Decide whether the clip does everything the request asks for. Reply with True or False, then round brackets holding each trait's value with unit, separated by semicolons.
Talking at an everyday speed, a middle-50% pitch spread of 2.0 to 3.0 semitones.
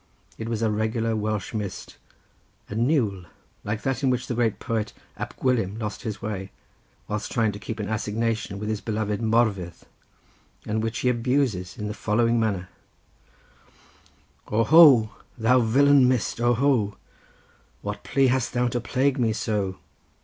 True (155 wpm; 2.5 semitones)